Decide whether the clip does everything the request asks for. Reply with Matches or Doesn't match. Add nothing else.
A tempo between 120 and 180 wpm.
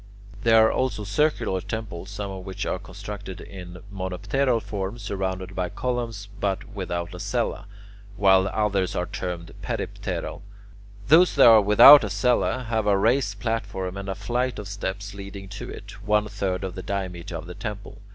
Matches